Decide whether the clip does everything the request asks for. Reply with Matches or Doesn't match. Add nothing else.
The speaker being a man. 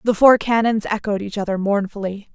Doesn't match